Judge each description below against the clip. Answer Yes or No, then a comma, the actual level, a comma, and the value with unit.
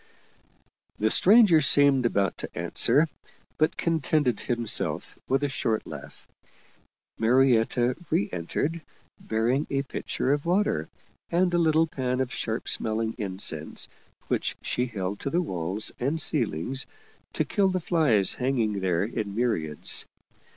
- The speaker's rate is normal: No, slow, 130 wpm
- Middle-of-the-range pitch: No, low, 125 Hz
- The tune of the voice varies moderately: No, wide, 6.1 semitones